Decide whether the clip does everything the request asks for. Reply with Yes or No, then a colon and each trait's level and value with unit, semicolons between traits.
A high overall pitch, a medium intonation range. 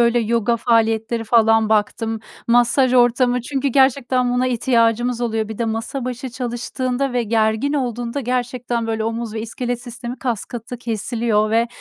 No: high, 235 Hz; narrow, 1.7 semitones